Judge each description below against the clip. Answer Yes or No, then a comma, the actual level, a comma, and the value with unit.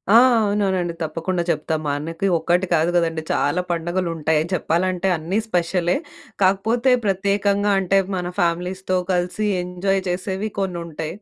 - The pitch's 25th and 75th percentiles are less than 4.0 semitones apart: Yes, narrow, 2.4 semitones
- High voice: No, medium, 180 Hz